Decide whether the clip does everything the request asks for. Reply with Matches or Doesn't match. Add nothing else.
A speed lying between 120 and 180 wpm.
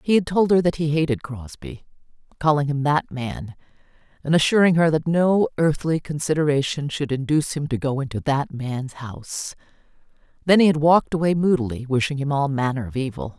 Matches